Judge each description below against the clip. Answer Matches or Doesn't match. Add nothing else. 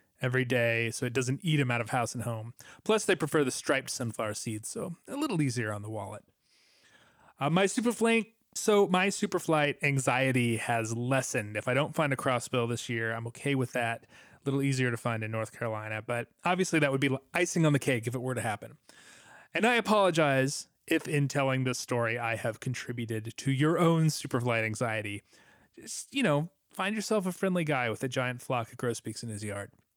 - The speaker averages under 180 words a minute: Doesn't match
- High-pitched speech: Doesn't match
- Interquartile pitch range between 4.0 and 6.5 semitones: Matches